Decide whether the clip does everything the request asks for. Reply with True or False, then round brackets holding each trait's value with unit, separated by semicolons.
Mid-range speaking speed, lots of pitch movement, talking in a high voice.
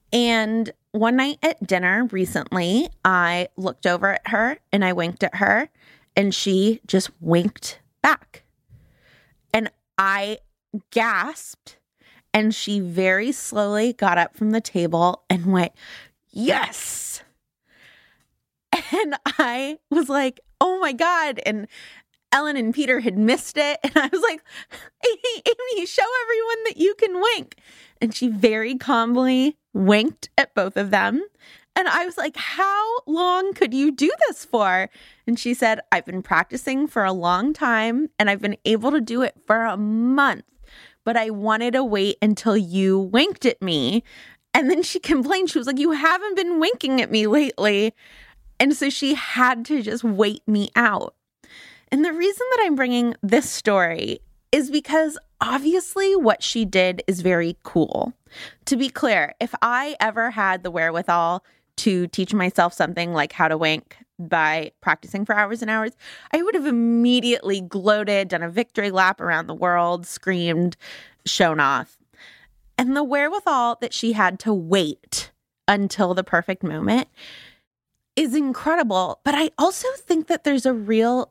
True (155 wpm; 7.1 semitones; 230 Hz)